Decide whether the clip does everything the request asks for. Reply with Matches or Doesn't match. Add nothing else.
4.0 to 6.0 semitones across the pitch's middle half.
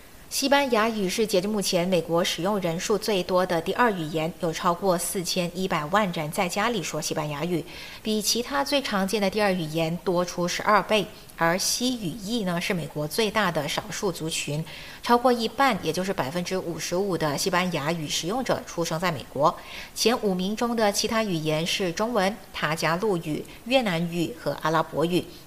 Matches